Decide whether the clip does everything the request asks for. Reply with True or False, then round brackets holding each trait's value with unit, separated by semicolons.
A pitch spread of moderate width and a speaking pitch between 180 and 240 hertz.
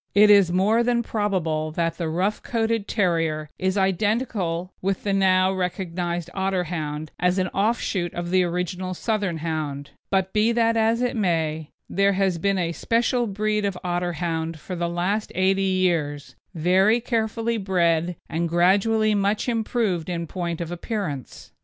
True (3.7 semitones; 185 Hz)